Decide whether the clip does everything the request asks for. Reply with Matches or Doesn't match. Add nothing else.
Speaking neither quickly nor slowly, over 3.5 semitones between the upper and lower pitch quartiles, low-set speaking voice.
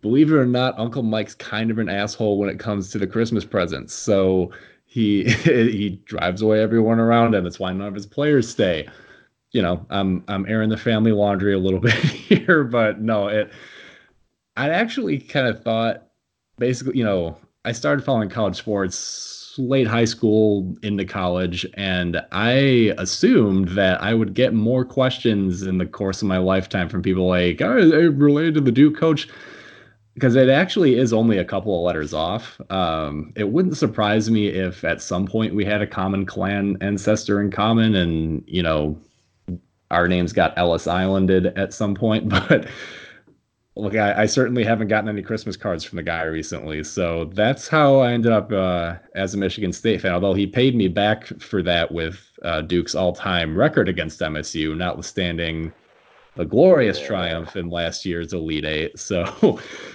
Matches